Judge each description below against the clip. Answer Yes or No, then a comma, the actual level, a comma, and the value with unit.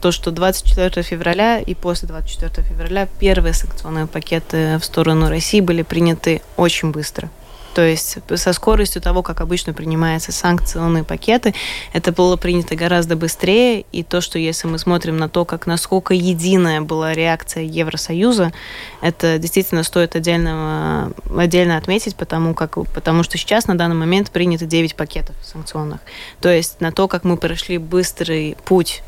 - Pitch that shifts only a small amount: Yes, narrow, 1.8 semitones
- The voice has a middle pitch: Yes, medium, 170 Hz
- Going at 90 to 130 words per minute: No, average, 155 wpm